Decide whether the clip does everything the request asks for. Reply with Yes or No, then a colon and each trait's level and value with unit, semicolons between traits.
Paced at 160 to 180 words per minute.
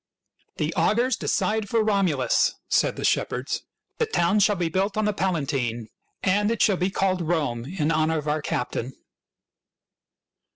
Yes: average, 170 wpm